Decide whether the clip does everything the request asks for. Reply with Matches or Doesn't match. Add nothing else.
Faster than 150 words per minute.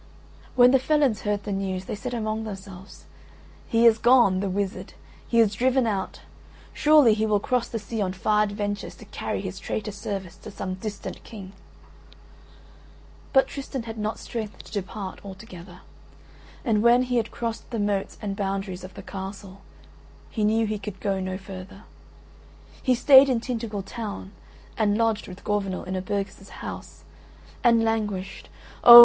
Matches